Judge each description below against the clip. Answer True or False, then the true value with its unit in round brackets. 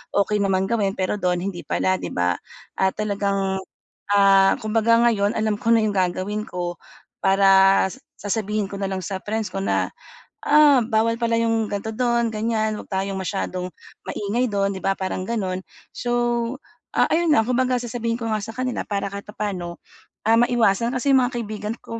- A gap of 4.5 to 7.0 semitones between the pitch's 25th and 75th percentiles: False (2.9 semitones)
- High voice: True (210 Hz)